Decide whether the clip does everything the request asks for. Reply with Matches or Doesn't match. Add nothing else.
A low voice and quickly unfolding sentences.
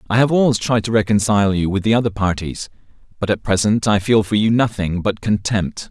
Matches